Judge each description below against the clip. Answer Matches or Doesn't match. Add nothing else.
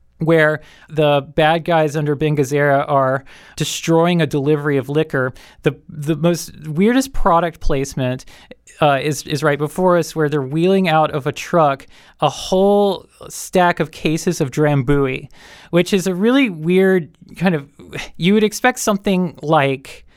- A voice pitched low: Doesn't match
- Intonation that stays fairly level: Doesn't match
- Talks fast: Doesn't match